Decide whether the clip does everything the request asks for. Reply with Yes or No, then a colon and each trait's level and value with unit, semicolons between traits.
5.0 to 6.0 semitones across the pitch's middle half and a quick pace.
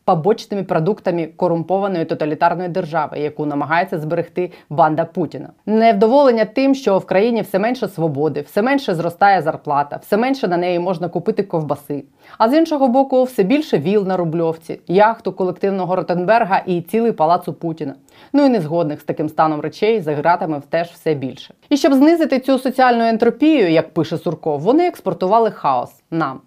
Yes: wide, 5.5 semitones; fast, 160 wpm